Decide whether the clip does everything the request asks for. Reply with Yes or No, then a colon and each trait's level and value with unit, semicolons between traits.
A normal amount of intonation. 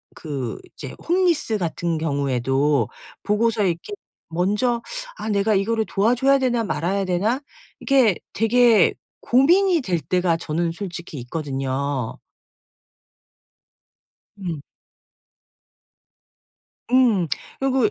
No: wide, 6.7 semitones